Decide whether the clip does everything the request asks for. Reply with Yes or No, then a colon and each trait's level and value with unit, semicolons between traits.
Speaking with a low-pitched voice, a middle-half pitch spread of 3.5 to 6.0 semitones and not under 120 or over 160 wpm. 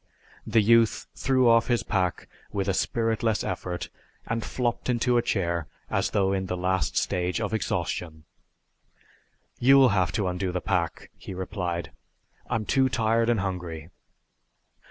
Yes: low, 100 Hz; average, 4.2 semitones; average, 145 wpm